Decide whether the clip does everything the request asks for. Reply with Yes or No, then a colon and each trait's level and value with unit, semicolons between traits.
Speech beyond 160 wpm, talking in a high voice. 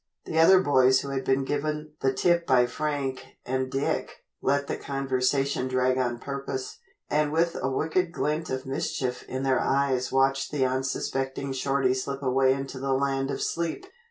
No: average, 170 wpm; low, 135 Hz